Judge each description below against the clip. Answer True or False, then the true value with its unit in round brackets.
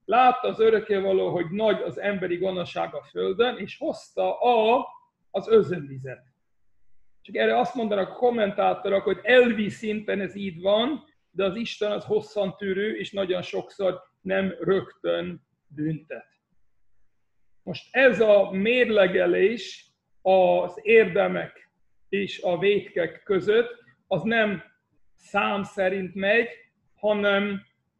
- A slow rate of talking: False (115 wpm)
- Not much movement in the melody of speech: False (3.5 semitones)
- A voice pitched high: True (200 Hz)